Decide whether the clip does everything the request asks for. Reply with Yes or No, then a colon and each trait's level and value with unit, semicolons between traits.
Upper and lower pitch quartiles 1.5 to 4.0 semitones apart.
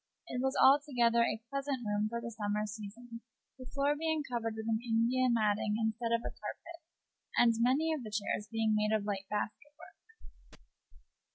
Yes: average, 3.4 semitones